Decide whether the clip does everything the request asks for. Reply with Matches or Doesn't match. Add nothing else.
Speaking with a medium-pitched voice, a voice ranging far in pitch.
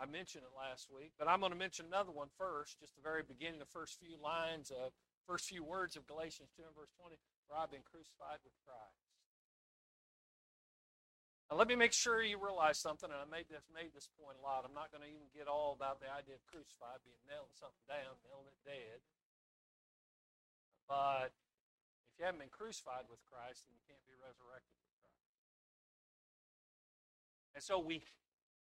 Doesn't match